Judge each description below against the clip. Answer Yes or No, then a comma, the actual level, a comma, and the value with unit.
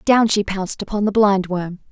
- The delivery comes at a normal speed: Yes, average, 190 wpm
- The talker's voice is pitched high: Yes, high, 200 Hz